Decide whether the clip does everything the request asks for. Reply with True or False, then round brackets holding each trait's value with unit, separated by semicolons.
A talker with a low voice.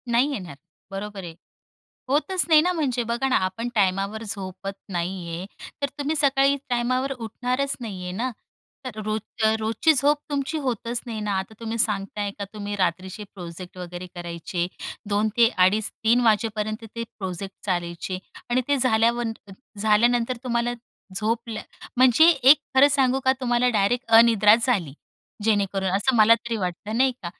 False (220 Hz)